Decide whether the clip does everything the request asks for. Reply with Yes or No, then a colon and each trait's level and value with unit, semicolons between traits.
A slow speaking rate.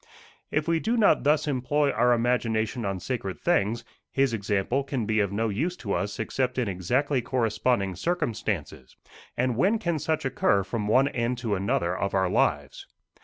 No: average, 170 wpm